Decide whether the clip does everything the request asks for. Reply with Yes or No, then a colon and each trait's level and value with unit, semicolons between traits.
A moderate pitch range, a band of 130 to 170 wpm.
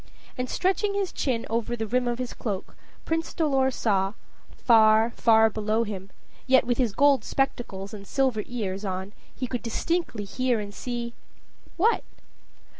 Yes: average, 3.7 semitones; average, 155 wpm